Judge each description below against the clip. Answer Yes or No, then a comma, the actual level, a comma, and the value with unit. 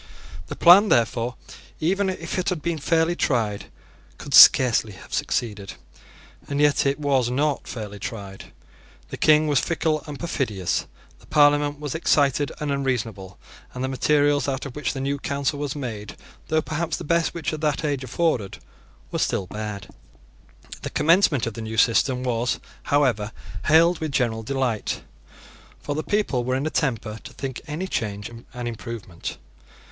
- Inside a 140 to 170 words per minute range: Yes, average, 160 wpm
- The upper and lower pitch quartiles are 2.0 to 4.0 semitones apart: No, average, 4.8 semitones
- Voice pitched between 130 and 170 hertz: Yes, medium, 140 Hz